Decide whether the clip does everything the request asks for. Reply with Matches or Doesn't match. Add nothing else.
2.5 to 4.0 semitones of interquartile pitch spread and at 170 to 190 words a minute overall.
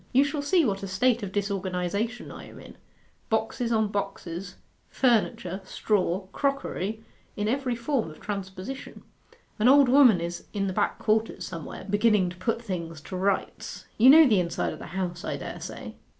Doesn't match